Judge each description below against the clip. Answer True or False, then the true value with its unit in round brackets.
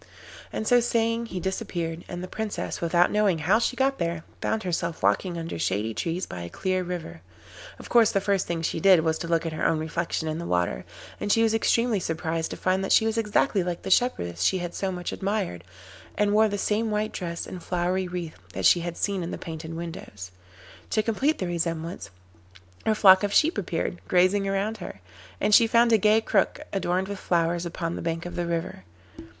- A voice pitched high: False (180 Hz)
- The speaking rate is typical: False (210 wpm)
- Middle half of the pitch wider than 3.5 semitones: True (4.0 semitones)